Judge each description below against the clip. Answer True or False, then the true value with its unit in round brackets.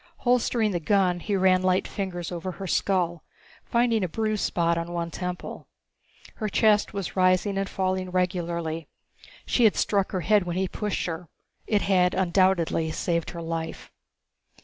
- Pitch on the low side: False (185 Hz)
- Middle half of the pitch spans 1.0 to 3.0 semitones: True (2.5 semitones)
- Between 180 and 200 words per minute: False (160 wpm)